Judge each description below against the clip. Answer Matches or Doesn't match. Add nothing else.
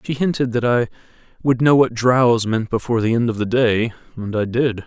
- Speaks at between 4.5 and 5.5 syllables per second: Matches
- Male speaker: Matches